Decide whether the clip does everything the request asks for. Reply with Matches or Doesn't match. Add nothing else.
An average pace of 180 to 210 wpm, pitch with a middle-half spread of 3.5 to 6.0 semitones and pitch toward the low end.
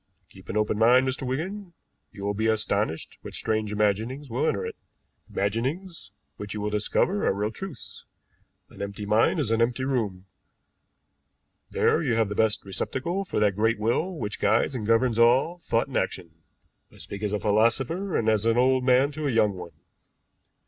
Matches